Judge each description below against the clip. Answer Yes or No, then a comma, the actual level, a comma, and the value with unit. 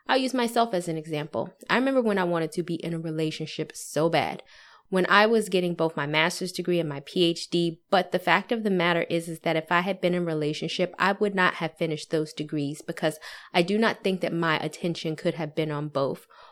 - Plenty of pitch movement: No, average, 2.7 semitones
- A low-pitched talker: No, medium, 170 Hz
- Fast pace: Yes, fast, 235 wpm